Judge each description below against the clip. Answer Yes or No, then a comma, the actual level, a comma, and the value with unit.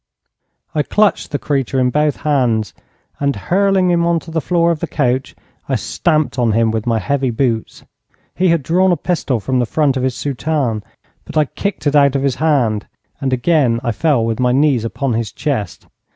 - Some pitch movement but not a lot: Yes, average, 4.7 semitones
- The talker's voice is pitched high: No, medium, 140 Hz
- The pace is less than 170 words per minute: No, average, 200 wpm